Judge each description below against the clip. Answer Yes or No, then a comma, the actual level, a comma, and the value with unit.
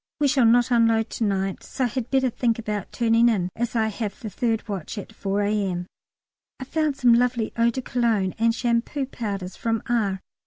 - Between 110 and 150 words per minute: No, average, 200 wpm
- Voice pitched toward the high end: Yes, high, 230 Hz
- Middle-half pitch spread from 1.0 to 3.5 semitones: Yes, average, 2.9 semitones